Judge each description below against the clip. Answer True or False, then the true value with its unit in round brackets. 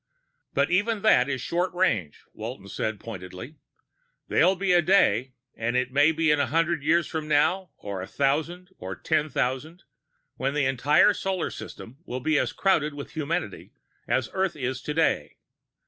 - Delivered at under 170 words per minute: True (160 wpm)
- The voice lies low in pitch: False (150 Hz)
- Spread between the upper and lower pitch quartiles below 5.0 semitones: False (5.3 semitones)